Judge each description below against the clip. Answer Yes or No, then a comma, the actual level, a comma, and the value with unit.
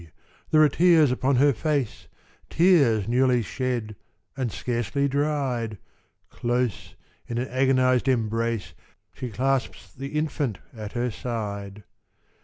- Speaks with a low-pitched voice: Yes, low, 125 Hz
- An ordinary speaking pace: No, slow, 115 wpm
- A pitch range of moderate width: Yes, average, 3.4 semitones